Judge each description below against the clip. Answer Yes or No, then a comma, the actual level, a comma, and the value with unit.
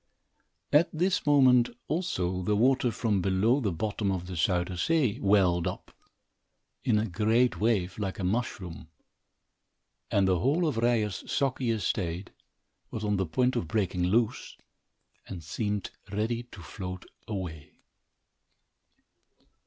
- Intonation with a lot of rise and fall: No, average, 4.8 semitones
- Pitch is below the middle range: Yes, low, 105 Hz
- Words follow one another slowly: Yes, slow, 130 wpm